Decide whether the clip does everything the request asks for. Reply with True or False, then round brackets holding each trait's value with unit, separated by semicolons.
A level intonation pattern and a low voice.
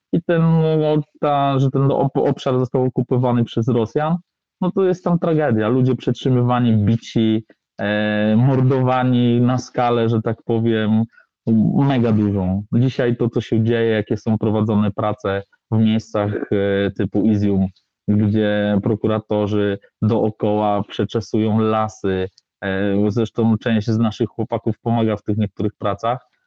False (3.2 semitones; 115 Hz)